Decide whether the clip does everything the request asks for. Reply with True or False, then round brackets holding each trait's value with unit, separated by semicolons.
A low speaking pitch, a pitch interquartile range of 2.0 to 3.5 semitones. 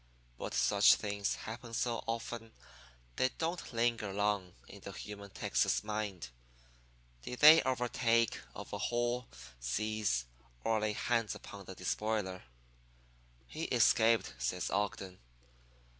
True (110 Hz; 2.7 semitones)